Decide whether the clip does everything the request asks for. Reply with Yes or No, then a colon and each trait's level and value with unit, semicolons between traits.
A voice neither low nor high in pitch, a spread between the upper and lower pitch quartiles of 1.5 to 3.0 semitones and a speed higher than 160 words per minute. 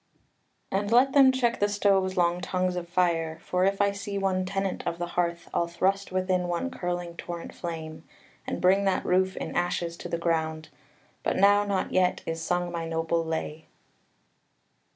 Yes: medium, 180 Hz; narrow, 2.4 semitones; average, 175 wpm